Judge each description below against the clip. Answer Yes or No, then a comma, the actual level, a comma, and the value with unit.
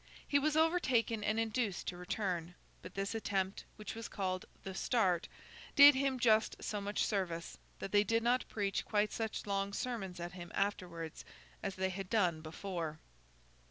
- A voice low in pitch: No, high, 200 Hz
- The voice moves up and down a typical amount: Yes, average, 3.7 semitones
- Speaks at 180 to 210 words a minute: No, average, 165 wpm